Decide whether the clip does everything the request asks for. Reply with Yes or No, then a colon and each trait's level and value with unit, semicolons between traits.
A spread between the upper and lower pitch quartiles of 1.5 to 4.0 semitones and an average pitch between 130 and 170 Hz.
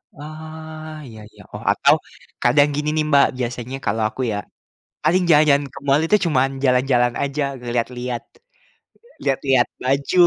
Yes: average, 3.6 semitones; medium, 140 Hz